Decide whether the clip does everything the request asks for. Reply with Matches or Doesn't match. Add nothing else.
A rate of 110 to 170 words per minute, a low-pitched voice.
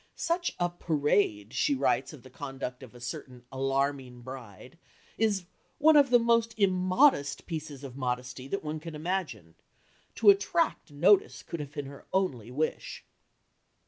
Doesn't match